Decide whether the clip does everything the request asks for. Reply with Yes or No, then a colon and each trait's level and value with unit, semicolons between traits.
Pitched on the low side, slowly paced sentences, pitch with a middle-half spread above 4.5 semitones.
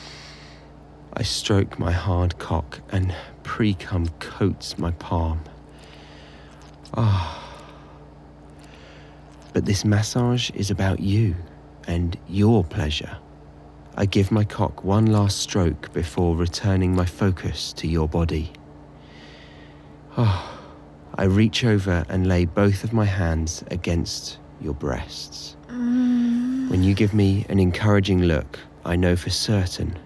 Yes: very low, 90 Hz; slow, 120 wpm; average, 5.3 semitones